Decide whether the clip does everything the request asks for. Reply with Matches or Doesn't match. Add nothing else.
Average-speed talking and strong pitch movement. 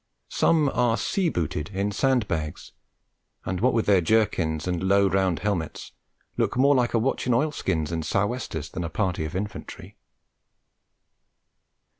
Matches